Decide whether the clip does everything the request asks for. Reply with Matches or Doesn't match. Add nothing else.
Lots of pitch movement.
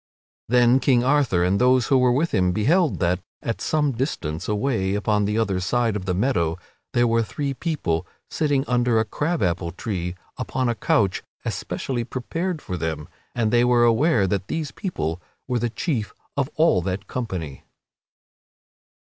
Matches